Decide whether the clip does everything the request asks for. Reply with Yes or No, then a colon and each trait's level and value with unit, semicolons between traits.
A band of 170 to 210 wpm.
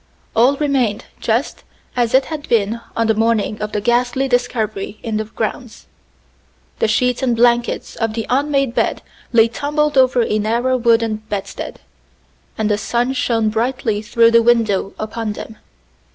No: average, 155 wpm